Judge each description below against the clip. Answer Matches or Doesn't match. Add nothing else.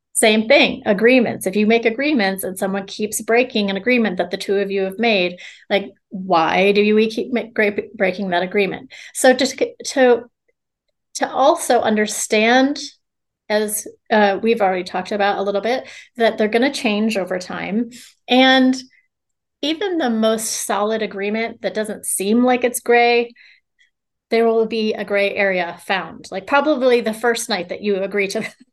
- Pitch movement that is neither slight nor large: Matches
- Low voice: Doesn't match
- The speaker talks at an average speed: Matches